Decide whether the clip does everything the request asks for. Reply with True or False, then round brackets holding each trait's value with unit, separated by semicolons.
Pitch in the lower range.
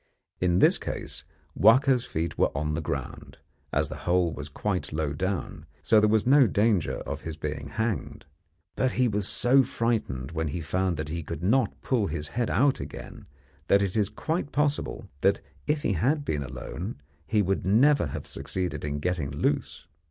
True (95 Hz)